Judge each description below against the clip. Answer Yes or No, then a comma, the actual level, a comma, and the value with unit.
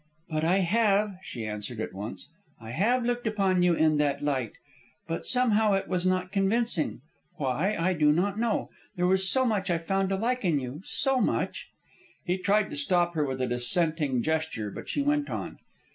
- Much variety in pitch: Yes, wide, 5.9 semitones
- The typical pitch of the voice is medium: Yes, medium, 180 Hz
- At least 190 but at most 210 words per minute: Yes, average, 195 wpm